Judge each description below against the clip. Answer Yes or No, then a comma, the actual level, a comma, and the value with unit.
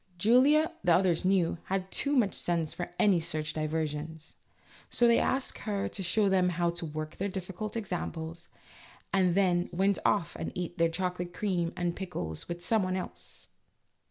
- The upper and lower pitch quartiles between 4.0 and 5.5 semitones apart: No, average, 2.8 semitones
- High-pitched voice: No, medium, 180 Hz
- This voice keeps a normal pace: Yes, average, 175 wpm